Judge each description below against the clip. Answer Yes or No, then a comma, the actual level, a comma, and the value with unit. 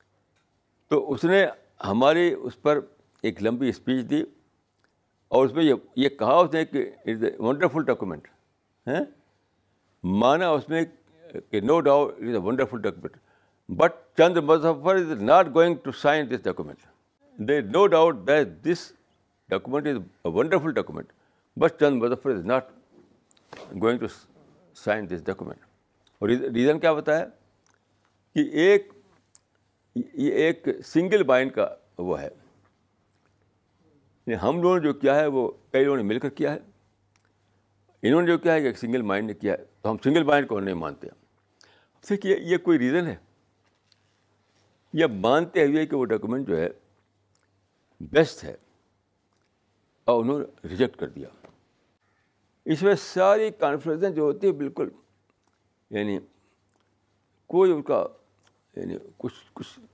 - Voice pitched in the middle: No, low, 130 Hz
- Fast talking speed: No, average, 145 wpm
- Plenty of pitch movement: Yes, wide, 8.1 semitones